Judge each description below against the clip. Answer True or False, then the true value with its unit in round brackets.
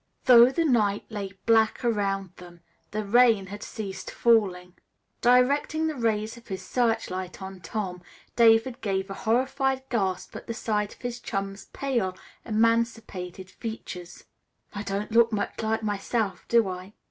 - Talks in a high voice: True (215 Hz)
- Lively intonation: False (3.3 semitones)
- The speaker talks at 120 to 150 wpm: True (145 wpm)